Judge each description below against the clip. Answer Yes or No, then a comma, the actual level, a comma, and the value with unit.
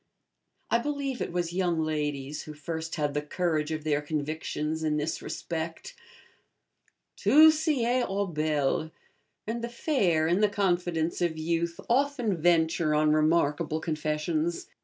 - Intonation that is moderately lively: Yes, average, 3.9 semitones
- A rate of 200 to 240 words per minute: No, average, 140 wpm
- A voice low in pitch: No, medium, 165 Hz